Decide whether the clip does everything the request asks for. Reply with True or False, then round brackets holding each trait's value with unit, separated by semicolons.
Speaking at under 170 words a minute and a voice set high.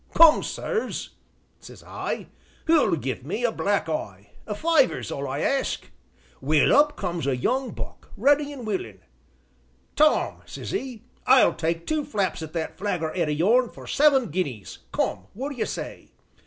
True (160 wpm; 210 Hz)